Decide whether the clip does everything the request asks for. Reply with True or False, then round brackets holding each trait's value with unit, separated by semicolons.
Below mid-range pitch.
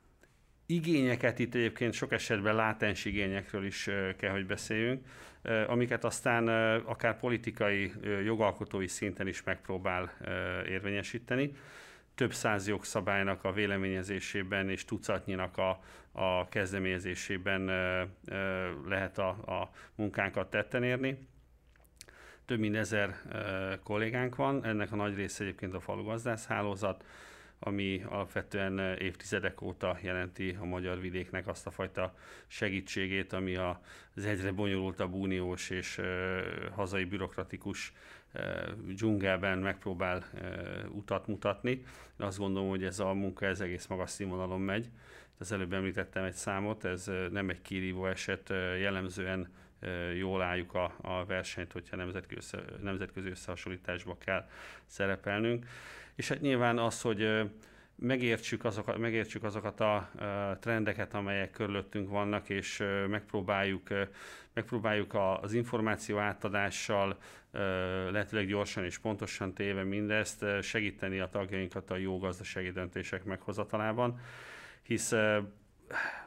True (100 Hz)